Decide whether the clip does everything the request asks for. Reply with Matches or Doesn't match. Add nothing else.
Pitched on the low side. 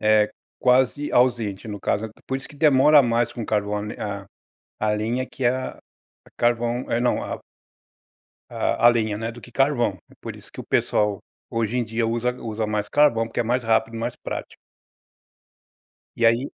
Matches